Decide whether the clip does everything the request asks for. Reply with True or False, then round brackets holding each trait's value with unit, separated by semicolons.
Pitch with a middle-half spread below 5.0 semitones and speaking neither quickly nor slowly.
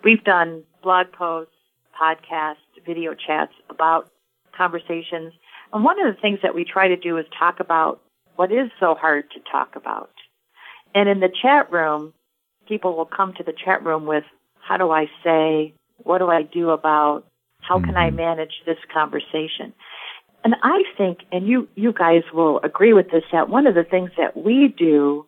True (3.0 semitones; 180 wpm)